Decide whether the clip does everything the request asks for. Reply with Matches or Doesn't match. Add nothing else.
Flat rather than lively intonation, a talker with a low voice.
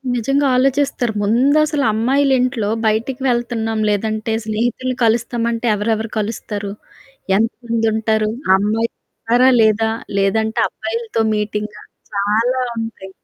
Doesn't match